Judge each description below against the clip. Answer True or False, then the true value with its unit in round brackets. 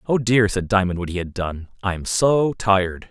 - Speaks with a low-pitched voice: True (100 Hz)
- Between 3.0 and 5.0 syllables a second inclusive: True (4.6 syllables/s)